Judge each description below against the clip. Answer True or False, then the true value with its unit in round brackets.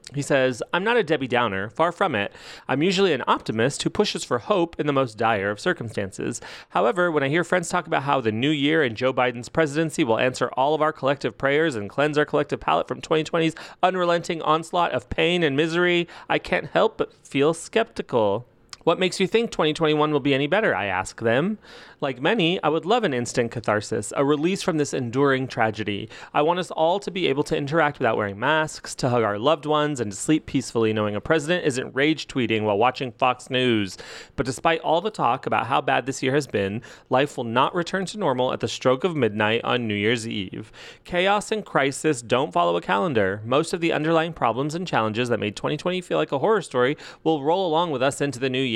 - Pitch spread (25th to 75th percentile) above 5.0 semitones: True (5.4 semitones)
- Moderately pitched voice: True (145 Hz)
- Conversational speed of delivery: False (220 wpm)